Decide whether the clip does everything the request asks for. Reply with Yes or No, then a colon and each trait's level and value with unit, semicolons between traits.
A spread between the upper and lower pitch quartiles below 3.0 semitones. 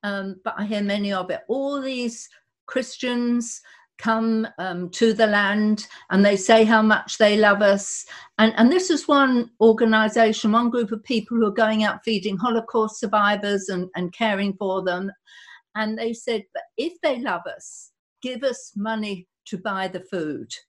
Yes: narrow, 2.5 semitones